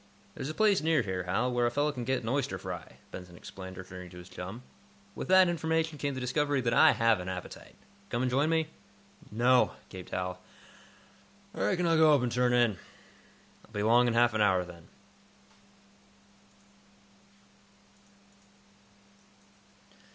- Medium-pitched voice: No, low, 120 Hz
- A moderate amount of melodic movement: No, wide, 7.4 semitones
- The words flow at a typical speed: Yes, average, 160 wpm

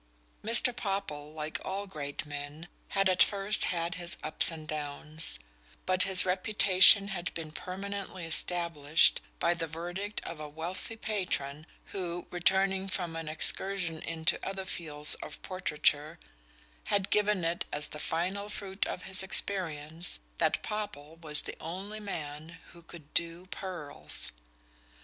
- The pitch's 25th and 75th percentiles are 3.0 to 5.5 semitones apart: Yes, average, 3.6 semitones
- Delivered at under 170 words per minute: Yes, average, 140 wpm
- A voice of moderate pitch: Yes, medium, 175 Hz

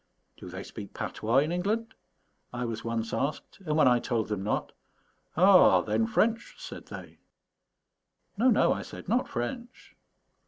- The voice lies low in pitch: Yes, low, 125 Hz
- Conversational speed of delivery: Yes, average, 155 wpm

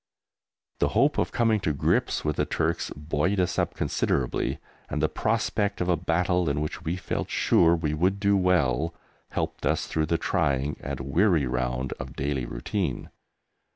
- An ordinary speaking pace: Yes, average, 170 wpm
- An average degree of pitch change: Yes, average, 4.6 semitones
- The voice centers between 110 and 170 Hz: No, very low, 80 Hz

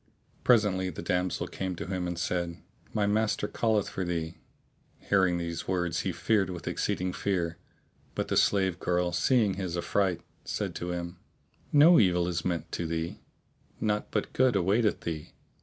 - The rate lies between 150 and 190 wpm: Yes, average, 160 wpm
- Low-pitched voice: Yes, very low, 90 Hz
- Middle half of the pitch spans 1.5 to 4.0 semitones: Yes, average, 2.8 semitones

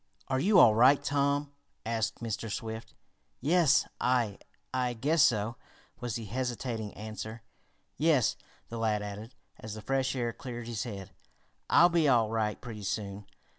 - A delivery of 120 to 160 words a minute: Yes, average, 150 wpm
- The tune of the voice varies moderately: Yes, average, 3.3 semitones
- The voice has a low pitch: Yes, low, 115 Hz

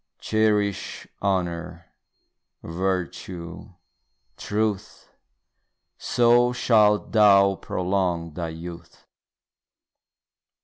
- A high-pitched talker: No, very low, 95 Hz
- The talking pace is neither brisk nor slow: No, slow, 55 wpm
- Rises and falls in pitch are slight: No, average, 3.6 semitones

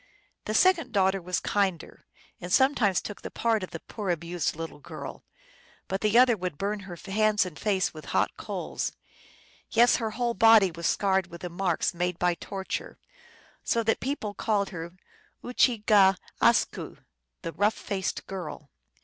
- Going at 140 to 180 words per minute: Yes, average, 160 wpm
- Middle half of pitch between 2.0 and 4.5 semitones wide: Yes, average, 3.6 semitones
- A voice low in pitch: No, high, 195 Hz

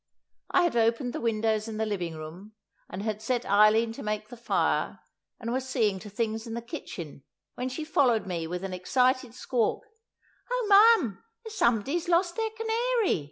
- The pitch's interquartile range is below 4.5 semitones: No, average, 4.9 semitones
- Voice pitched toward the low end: No, high, 230 Hz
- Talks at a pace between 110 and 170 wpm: No, average, 185 wpm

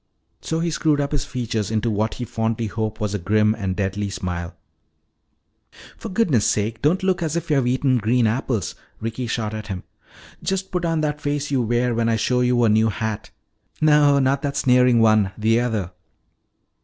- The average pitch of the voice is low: Yes, low, 120 Hz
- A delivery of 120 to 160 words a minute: No, average, 190 wpm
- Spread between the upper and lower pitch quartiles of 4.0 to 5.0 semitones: Yes, average, 4.7 semitones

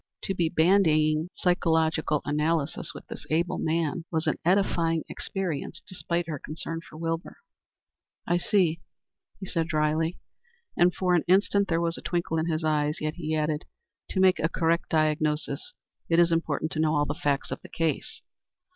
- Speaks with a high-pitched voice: No, medium, 165 Hz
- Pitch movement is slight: Yes, narrow, 2.0 semitones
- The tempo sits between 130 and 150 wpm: No, average, 170 wpm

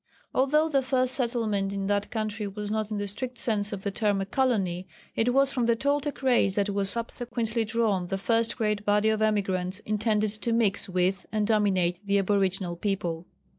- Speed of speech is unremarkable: Yes, average, 190 wpm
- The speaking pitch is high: Yes, high, 210 Hz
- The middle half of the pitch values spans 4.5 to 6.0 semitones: No, average, 2.9 semitones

